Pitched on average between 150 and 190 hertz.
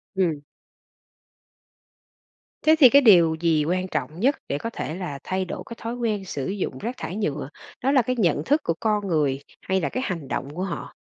Yes: medium, 185 Hz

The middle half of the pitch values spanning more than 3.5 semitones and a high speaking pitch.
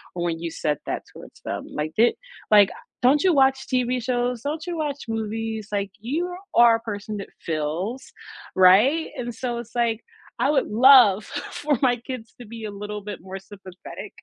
Yes: average, 4.2 semitones; high, 230 Hz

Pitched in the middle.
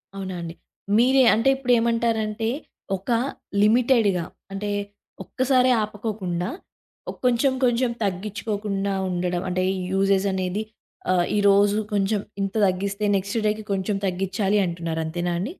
No: high, 200 Hz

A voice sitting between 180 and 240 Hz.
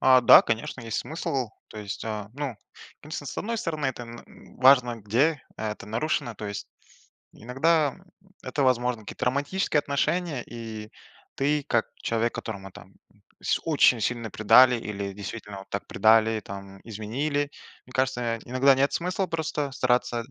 No: low, 125 Hz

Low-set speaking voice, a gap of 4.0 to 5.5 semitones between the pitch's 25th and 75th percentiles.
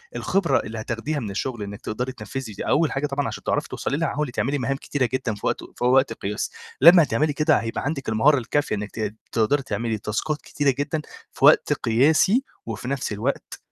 Yes: low, 130 Hz; average, 4.7 semitones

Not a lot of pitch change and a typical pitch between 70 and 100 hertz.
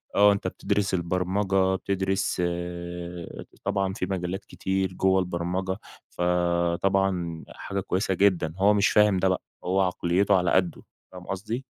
Yes: narrow, 1.5 semitones; very low, 95 Hz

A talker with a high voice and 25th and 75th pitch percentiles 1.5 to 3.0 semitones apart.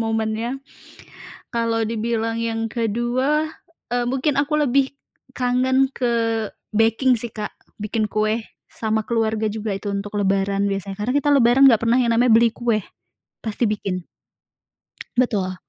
Yes: high, 225 Hz; narrow, 2.4 semitones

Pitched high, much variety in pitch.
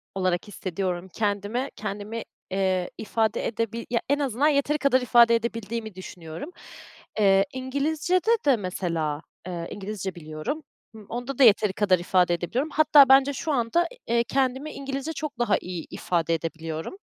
Yes: high, 220 Hz; wide, 6.5 semitones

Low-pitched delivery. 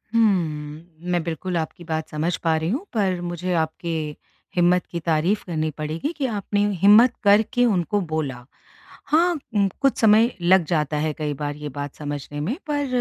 No: medium, 175 Hz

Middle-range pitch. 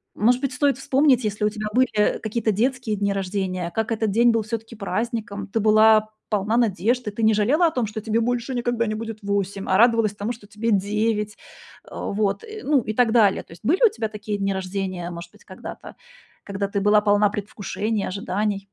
No: high, 215 Hz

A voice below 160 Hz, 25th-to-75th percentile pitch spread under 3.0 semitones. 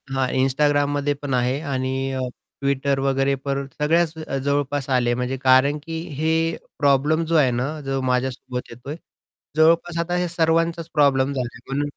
Yes: medium, 140 Hz; narrow, 2.4 semitones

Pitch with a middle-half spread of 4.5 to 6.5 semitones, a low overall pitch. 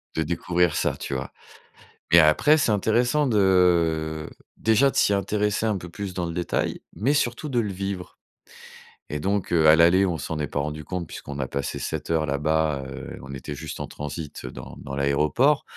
Yes: average, 5.0 semitones; very low, 85 Hz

